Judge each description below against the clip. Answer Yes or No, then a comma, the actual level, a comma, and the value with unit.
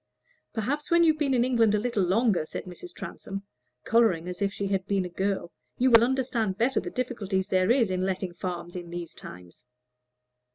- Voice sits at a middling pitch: No, high, 200 Hz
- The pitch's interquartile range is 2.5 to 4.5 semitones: No, average, 4.9 semitones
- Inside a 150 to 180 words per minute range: No, average, 190 wpm